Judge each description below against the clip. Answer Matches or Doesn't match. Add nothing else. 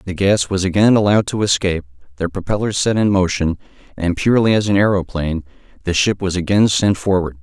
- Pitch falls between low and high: Doesn't match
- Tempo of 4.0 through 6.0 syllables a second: Doesn't match